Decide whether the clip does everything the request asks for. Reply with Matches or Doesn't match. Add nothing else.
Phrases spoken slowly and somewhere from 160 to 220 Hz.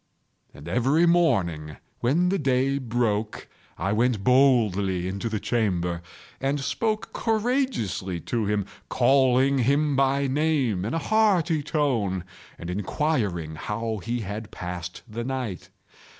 Doesn't match